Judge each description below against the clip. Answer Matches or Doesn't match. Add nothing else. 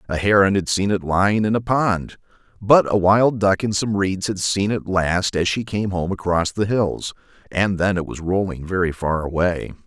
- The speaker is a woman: Doesn't match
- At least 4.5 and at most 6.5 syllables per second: Matches